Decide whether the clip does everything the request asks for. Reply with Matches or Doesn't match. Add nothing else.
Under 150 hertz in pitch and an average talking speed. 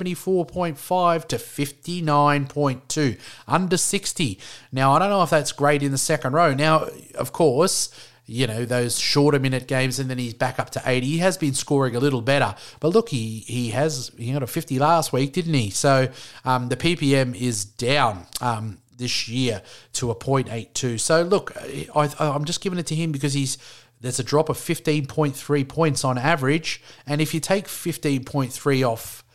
Matches